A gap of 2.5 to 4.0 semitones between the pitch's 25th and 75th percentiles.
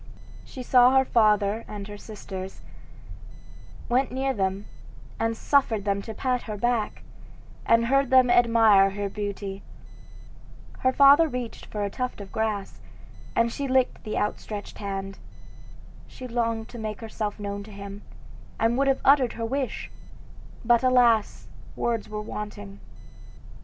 Yes: average, 3.5 semitones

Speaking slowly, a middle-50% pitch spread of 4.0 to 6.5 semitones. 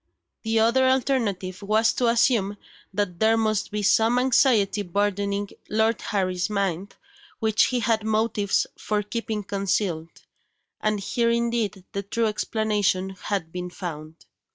No: slow, 130 wpm; narrow, 2.5 semitones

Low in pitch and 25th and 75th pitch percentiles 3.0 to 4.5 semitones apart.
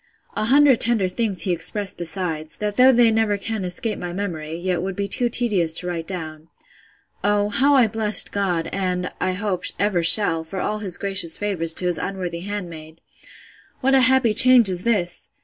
No: high, 195 Hz; average, 3.6 semitones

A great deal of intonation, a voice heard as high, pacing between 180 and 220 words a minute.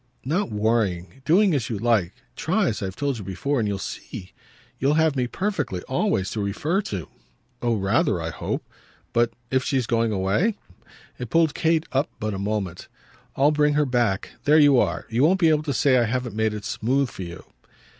No: wide, 6.1 semitones; low, 120 Hz; average, 195 wpm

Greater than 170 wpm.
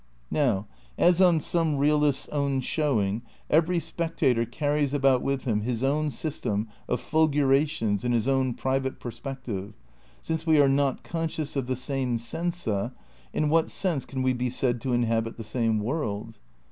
No: average, 165 wpm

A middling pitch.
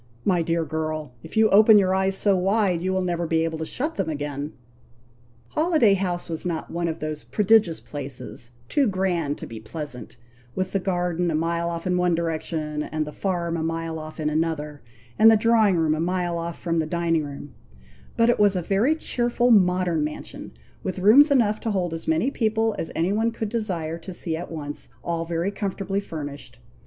Yes: medium, 170 Hz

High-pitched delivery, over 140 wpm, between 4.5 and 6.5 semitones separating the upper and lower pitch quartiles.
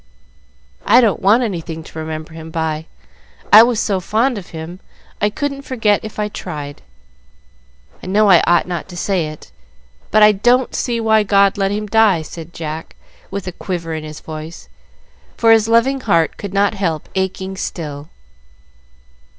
Yes: high, 195 Hz; average, 165 wpm; average, 4.9 semitones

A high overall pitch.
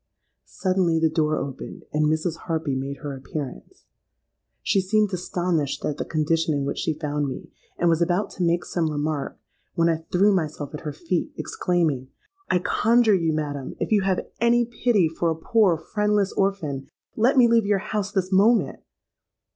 No: medium, 170 Hz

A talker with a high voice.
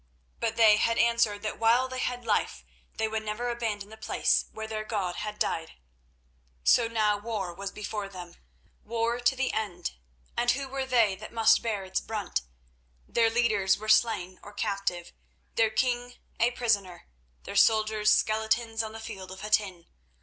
Yes: high, 220 Hz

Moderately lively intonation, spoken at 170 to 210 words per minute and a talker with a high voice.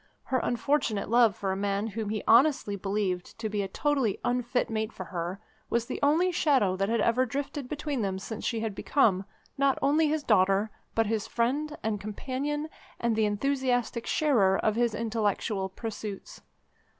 Yes: average, 4.7 semitones; average, 175 wpm; high, 225 Hz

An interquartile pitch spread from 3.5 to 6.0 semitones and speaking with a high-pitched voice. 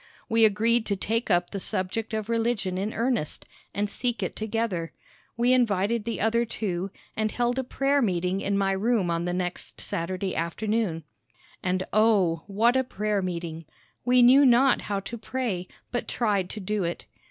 Yes: average, 4.0 semitones; high, 210 Hz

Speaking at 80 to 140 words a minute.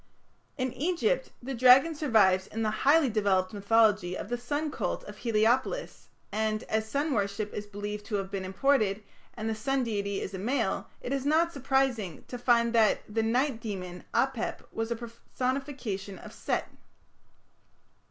No: average, 160 wpm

